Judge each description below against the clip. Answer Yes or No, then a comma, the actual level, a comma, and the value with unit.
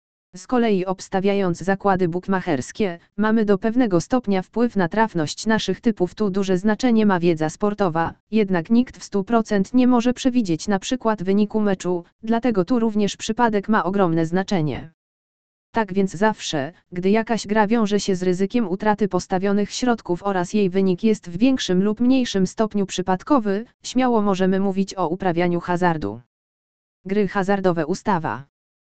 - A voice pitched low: No, high, 200 Hz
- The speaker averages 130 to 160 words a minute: Yes, average, 145 wpm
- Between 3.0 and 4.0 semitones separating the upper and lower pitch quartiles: Yes, average, 3.3 semitones